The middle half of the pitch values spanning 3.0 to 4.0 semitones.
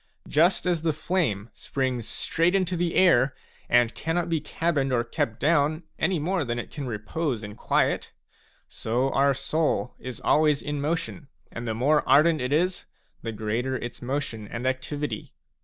No: average, 5.2 semitones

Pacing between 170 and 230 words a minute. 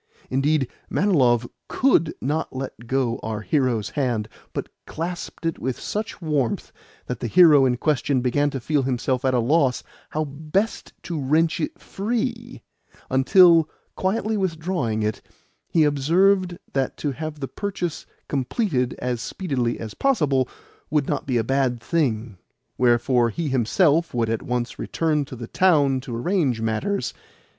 No: average, 150 wpm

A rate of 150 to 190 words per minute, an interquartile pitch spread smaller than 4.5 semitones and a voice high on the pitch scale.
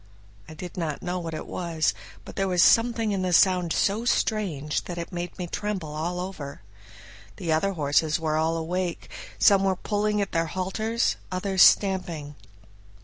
No: average, 170 wpm; average, 3.3 semitones; medium, 180 Hz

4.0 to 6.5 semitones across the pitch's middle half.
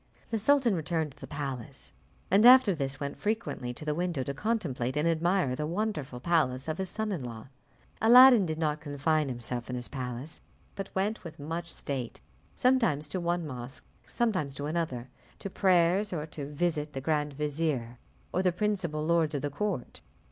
Yes: average, 5.1 semitones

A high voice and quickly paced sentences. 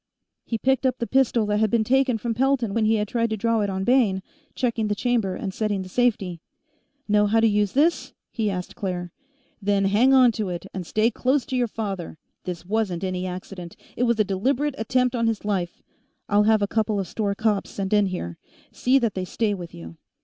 Yes: high, 215 Hz; fast, 215 wpm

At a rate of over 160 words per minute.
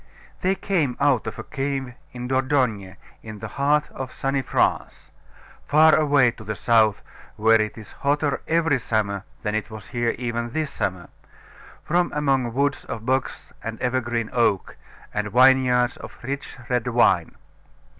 No: average, 155 wpm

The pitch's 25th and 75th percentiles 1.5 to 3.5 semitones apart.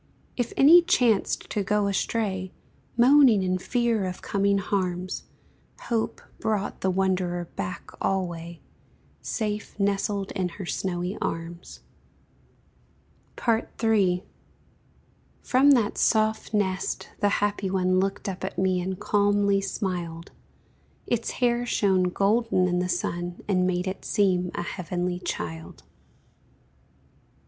Yes: narrow, 2.6 semitones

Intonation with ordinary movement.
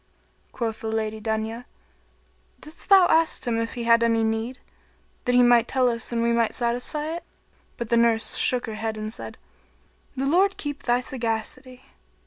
No: narrow, 2.3 semitones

